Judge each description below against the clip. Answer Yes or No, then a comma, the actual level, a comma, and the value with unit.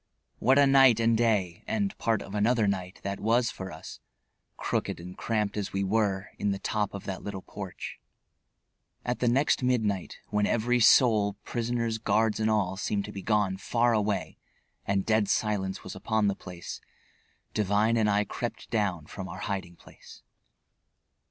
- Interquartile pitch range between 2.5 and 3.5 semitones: Yes, average, 2.9 semitones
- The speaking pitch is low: Yes, low, 105 Hz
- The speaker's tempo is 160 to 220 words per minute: Yes, average, 170 wpm